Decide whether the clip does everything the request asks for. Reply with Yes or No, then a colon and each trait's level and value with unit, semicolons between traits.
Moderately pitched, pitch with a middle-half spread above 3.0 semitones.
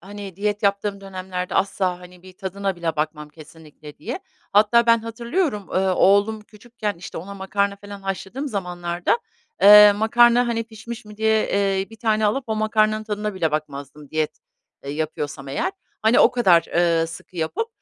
No: high, 200 Hz; average, 3.8 semitones